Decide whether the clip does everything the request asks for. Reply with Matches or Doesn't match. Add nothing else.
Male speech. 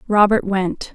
Doesn't match